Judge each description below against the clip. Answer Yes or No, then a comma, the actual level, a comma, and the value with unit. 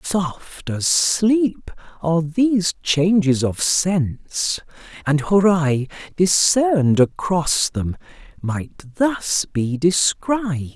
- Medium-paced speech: No, slow, 95 wpm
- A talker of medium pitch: Yes, medium, 170 Hz